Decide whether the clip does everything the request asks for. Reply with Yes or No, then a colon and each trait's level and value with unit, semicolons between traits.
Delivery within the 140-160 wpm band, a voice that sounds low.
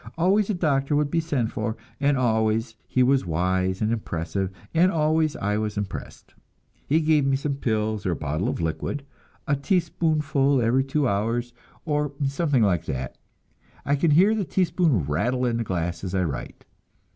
No: average, 175 wpm; low, 130 Hz